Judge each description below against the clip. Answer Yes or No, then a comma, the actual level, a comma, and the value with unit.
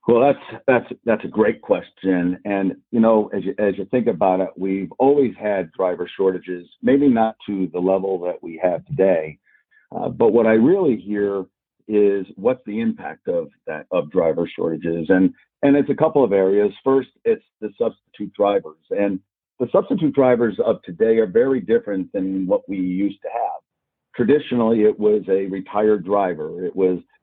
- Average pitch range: No, wide, 5.9 semitones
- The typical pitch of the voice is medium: No, low, 105 Hz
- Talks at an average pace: Yes, average, 180 wpm